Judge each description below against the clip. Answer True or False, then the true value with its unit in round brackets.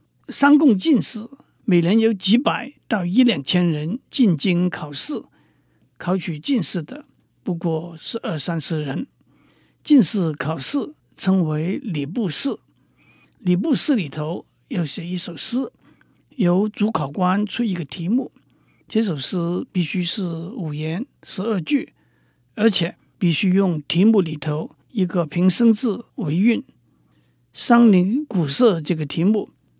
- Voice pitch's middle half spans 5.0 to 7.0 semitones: True (5.3 semitones)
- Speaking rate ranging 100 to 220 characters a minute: True (185 characters per minute)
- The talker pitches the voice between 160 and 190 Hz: True (185 Hz)